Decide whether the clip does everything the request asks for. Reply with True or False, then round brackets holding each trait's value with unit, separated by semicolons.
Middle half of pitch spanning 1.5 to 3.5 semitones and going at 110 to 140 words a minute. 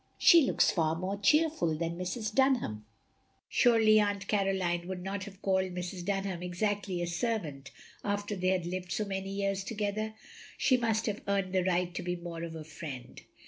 False (2.9 semitones; 180 wpm)